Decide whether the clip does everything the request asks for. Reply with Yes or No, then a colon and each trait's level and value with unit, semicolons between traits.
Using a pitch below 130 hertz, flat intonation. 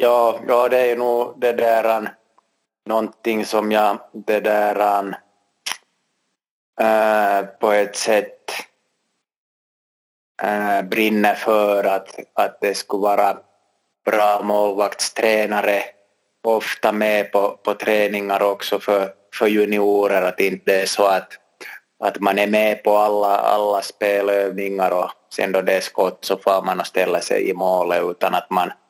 Yes: low, 105 Hz; narrow, 1.4 semitones